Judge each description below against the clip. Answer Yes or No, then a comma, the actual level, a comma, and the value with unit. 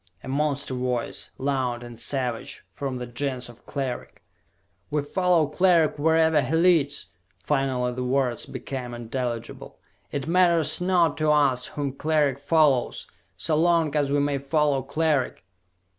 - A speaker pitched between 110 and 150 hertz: Yes, medium, 140 Hz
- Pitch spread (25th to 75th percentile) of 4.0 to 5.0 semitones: No, average, 3.6 semitones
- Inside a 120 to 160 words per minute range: Yes, average, 140 wpm